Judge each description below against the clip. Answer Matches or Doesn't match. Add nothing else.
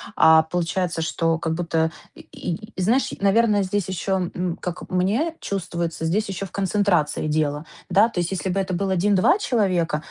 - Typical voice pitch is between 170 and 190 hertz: Matches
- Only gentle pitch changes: Doesn't match